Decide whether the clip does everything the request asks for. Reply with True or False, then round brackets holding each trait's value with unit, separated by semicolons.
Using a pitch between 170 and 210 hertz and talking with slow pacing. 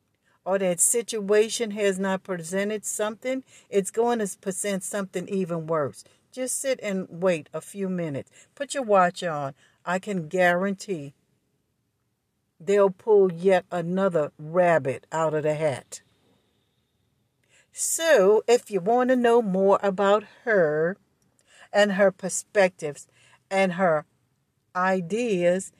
True (190 Hz; 120 wpm)